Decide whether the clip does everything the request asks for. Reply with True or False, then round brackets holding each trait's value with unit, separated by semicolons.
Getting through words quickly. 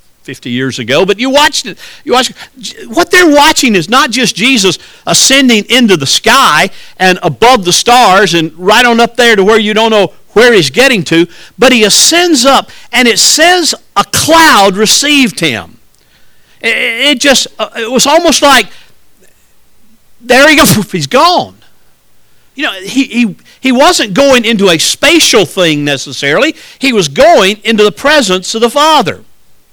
False (165 wpm)